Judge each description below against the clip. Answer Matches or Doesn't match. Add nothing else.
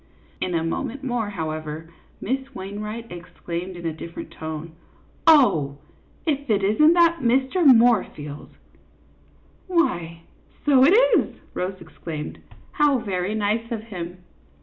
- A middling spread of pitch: Doesn't match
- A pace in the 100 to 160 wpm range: Matches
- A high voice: Matches